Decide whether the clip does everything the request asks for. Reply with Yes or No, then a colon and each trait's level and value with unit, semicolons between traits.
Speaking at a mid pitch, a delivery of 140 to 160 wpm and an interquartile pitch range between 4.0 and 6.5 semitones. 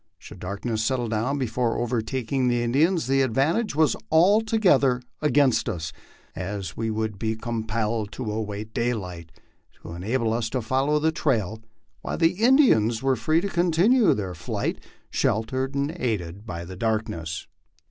No: low, 120 Hz; average, 150 wpm; average, 4.8 semitones